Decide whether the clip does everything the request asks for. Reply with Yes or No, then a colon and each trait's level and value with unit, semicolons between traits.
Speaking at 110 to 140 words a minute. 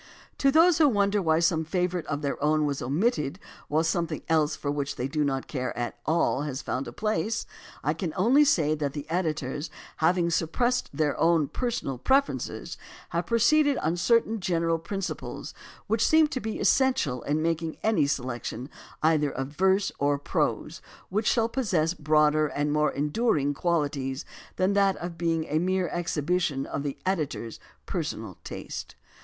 No: average, 170 wpm